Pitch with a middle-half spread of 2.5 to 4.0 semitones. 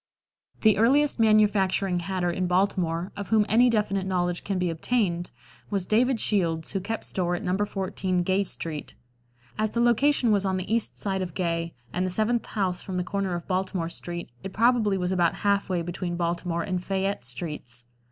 Yes: average, 3.0 semitones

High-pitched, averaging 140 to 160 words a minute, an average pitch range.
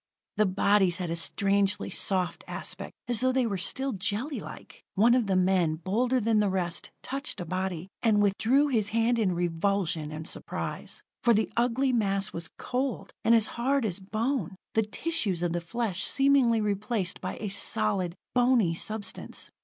No: high, 205 Hz; average, 170 wpm; average, 4.5 semitones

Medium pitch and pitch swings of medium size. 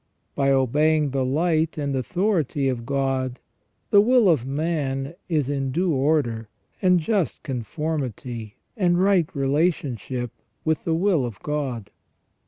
Yes: medium, 145 Hz; average, 4.1 semitones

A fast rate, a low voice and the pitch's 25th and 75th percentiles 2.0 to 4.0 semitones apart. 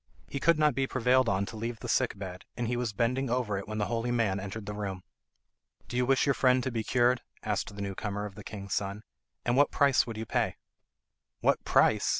Yes: fast, 235 wpm; low, 115 Hz; average, 3.6 semitones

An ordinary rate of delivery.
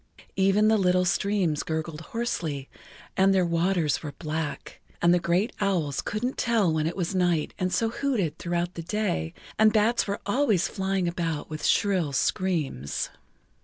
Yes: average, 160 wpm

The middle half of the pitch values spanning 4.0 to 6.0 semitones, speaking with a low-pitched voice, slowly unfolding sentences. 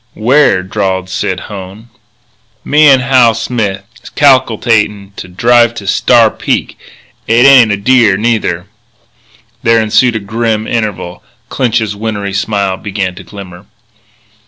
No: average, 3.3 semitones; low, 110 Hz; slow, 125 wpm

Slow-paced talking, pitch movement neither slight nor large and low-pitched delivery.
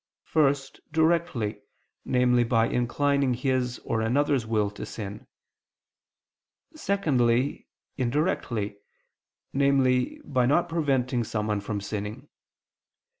Yes: slow, 90 wpm; average, 3.9 semitones; low, 125 Hz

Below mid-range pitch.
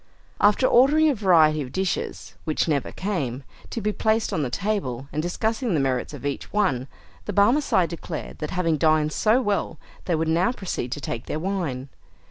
No: medium, 170 Hz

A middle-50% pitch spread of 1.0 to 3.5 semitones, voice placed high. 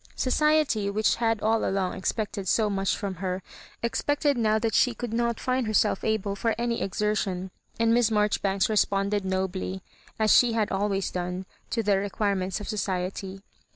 Yes: average, 2.8 semitones; high, 210 Hz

